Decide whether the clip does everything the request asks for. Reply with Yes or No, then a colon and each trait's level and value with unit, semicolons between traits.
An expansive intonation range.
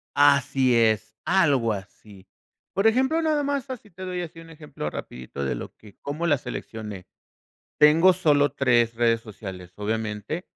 Yes: wide, 7.9 semitones